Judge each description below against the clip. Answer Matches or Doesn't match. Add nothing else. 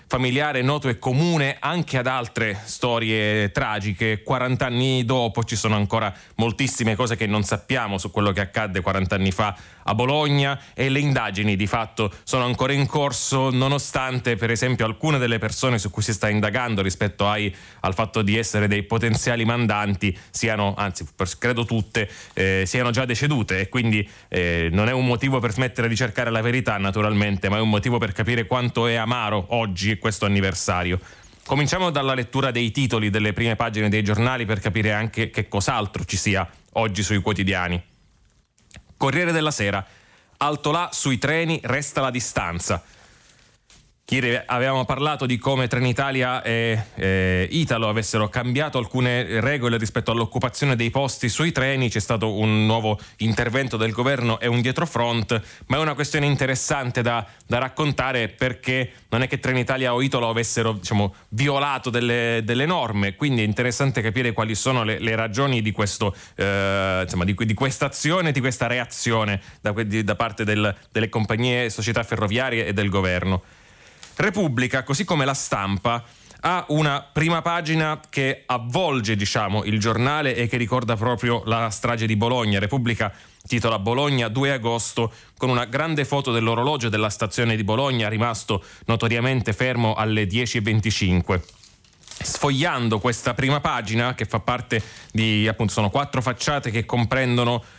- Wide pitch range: Doesn't match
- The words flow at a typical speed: Matches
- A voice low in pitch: Matches